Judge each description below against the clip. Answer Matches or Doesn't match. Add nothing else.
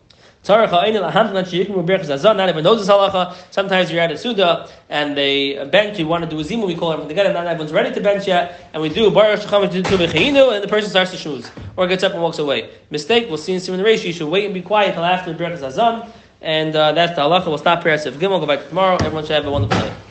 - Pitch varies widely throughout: Doesn't match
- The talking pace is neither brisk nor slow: Doesn't match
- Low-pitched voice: Doesn't match